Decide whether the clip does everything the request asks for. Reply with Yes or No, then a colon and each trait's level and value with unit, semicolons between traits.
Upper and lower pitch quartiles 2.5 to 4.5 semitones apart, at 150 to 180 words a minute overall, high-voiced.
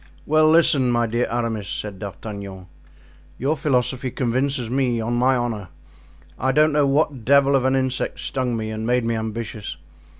No: average, 3.3 semitones; average, 165 wpm; low, 125 Hz